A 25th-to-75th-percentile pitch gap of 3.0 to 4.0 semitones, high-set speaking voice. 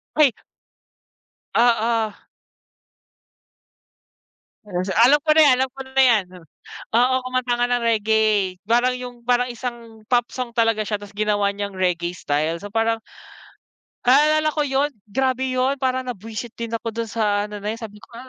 Yes: average, 3.4 semitones; high, 230 Hz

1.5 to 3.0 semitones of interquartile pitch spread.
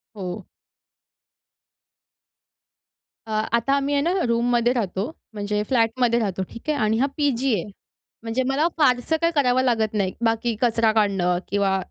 No: average, 3.7 semitones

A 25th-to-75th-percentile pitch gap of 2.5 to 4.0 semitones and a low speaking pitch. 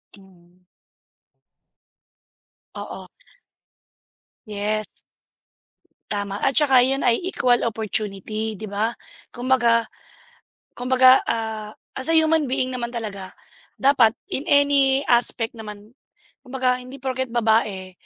No: average, 3.5 semitones; high, 235 Hz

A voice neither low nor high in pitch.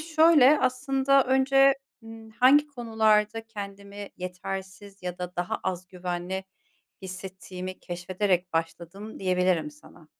No: high, 195 Hz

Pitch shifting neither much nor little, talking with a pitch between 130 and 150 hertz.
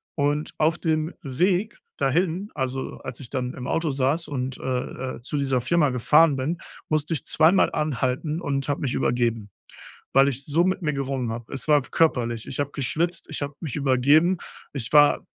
Yes: average, 3.5 semitones; medium, 140 Hz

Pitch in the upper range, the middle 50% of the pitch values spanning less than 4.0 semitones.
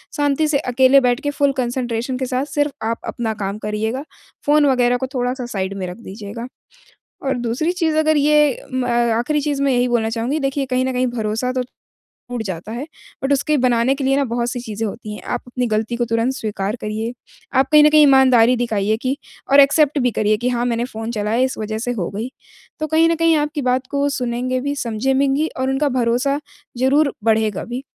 Yes: very high, 250 Hz; average, 3.5 semitones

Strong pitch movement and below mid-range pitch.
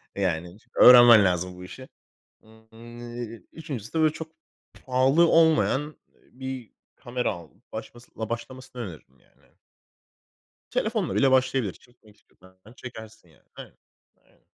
No: average, 4.2 semitones; low, 120 Hz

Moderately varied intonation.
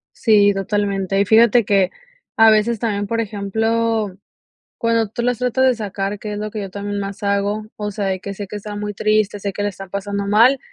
No: narrow, 1.9 semitones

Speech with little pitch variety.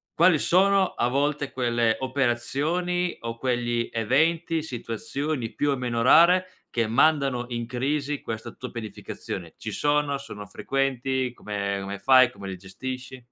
No: average, 4.0 semitones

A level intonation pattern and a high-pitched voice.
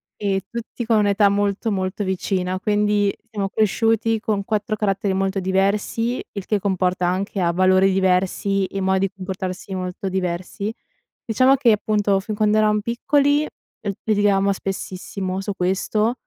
Yes: narrow, 2.1 semitones; high, 200 Hz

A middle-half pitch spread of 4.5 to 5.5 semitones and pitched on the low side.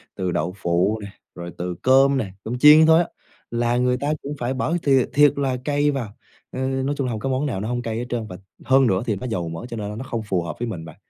Yes: average, 5.0 semitones; low, 120 Hz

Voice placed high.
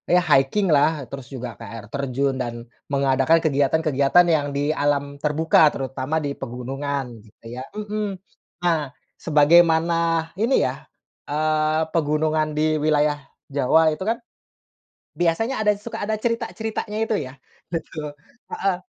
No: medium, 155 Hz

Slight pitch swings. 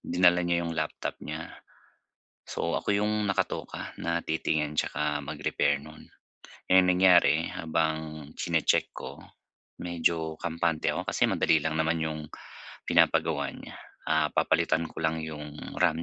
Yes: narrow, 1.7 semitones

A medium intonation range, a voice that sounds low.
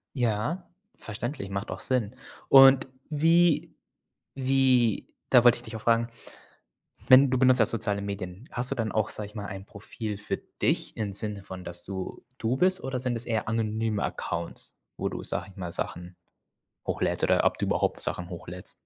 Yes: average, 4.3 semitones; low, 110 Hz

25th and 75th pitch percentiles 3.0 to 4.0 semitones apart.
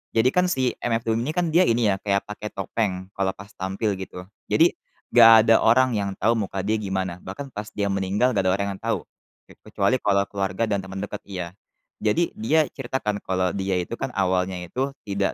Yes: average, 3.5 semitones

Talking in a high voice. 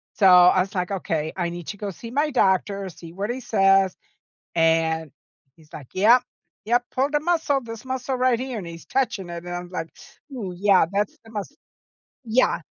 Yes: high, 195 Hz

